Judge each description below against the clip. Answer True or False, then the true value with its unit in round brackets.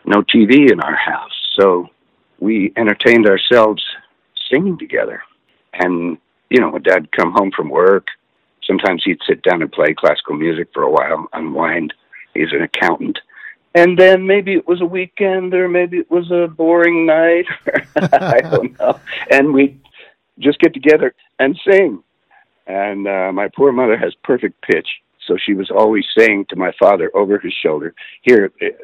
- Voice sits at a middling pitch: True (175 Hz)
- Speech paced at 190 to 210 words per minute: False (165 wpm)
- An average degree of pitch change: False (6.3 semitones)